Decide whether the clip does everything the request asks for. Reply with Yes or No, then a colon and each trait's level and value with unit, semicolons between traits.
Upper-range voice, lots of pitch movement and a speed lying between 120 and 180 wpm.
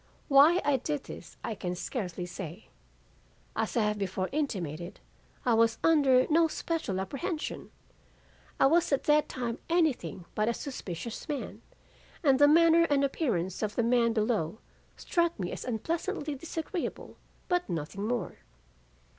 Yes: very high, 250 Hz; wide, 7.3 semitones; average, 145 wpm